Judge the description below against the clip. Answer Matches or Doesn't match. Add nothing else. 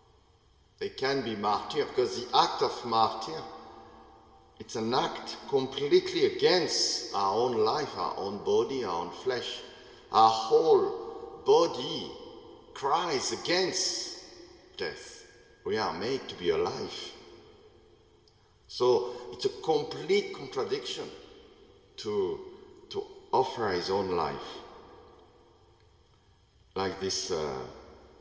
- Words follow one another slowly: Matches